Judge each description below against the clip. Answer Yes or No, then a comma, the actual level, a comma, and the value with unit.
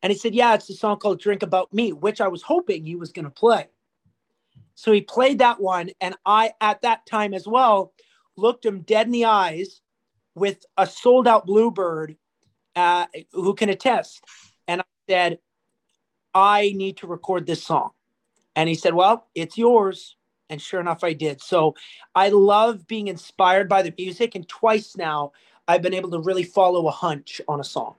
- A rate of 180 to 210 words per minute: Yes, average, 190 wpm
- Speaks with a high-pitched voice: Yes, high, 195 Hz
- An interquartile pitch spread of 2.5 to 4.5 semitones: Yes, average, 4.0 semitones